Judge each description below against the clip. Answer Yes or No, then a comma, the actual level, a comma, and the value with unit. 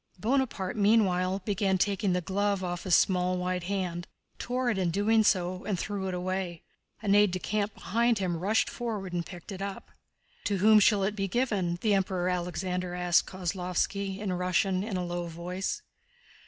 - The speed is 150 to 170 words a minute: No, average, 180 wpm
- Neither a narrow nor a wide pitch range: No, narrow, 2.2 semitones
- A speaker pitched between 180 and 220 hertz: Yes, high, 190 Hz